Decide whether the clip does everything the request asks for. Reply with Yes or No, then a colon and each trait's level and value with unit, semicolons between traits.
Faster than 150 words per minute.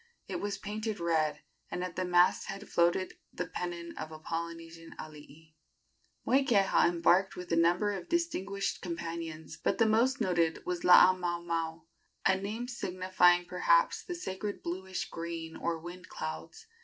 No: average, 145 wpm